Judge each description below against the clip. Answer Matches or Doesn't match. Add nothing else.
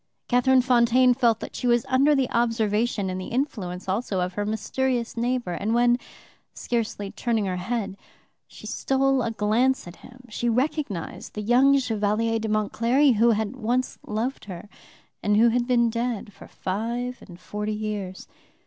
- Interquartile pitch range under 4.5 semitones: Matches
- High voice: Matches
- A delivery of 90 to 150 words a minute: Doesn't match